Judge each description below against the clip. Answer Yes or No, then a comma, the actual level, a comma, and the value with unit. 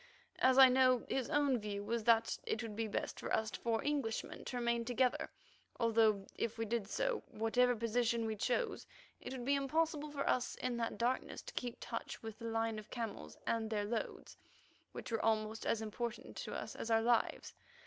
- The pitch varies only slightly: Yes, narrow, 2.2 semitones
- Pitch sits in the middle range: No, high, 230 Hz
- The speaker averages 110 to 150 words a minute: No, average, 195 wpm